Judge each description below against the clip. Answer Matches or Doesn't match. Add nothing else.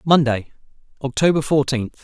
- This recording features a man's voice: Matches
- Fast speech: Doesn't match